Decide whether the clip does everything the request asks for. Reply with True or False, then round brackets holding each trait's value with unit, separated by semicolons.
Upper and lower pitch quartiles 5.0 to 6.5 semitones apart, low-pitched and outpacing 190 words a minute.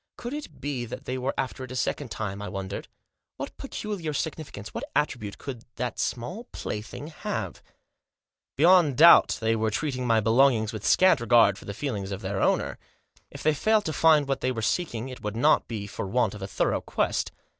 True (5.4 semitones; 125 Hz; 200 wpm)